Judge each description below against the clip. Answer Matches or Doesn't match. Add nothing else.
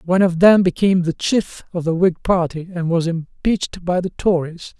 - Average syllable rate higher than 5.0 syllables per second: Matches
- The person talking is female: Doesn't match